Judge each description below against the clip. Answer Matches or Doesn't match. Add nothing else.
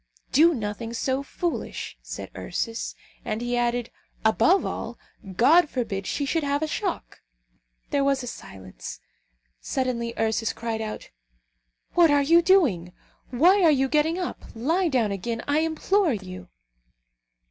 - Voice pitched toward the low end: Doesn't match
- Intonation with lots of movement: Matches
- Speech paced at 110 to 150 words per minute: Matches